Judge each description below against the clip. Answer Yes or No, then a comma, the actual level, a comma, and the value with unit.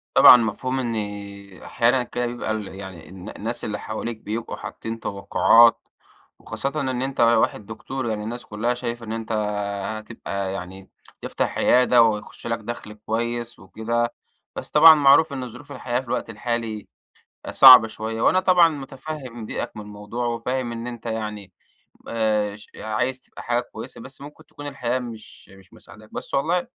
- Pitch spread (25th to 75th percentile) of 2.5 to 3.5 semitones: Yes, average, 2.8 semitones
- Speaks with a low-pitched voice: Yes, low, 115 Hz